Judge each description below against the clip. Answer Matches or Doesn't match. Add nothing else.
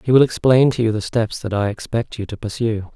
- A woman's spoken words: Doesn't match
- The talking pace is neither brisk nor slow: Doesn't match